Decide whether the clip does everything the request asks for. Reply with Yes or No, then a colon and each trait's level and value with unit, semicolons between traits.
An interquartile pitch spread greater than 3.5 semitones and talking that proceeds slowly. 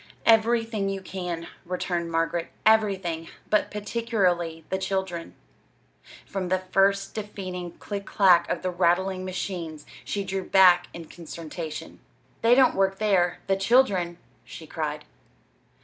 No: narrow, 2.5 semitones; slow, 125 wpm